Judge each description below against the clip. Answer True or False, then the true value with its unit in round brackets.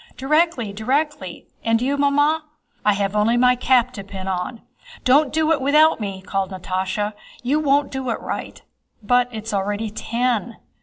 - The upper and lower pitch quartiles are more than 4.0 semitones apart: True (5.6 semitones)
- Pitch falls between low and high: False (240 Hz)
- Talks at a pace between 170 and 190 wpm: False (160 wpm)